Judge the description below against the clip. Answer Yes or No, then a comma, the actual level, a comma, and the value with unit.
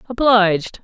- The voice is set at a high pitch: Yes, high, 210 Hz